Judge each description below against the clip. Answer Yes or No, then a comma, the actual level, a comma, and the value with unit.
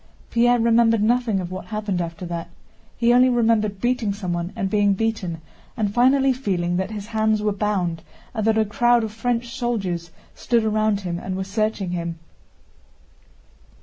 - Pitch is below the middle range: No, high, 215 Hz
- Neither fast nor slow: Yes, average, 165 wpm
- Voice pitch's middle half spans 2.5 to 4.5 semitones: Yes, average, 3.7 semitones